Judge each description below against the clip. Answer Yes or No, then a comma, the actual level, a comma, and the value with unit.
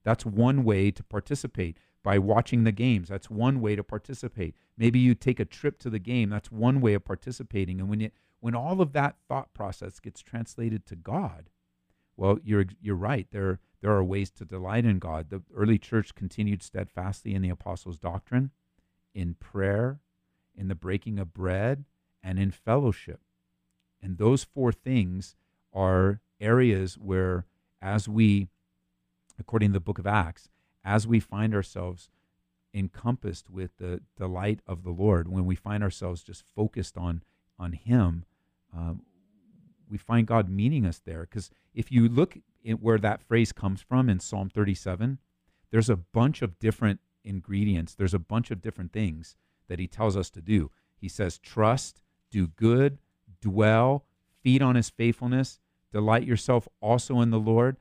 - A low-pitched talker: Yes, low, 105 Hz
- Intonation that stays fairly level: No, average, 3.8 semitones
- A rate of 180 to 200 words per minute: No, average, 165 wpm